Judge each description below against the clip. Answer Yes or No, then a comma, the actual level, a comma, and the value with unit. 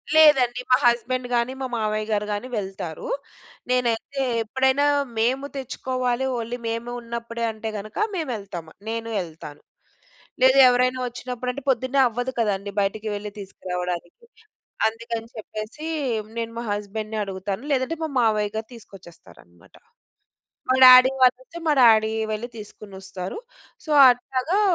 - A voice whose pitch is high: Yes, high, 230 Hz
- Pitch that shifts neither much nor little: Yes, average, 3.5 semitones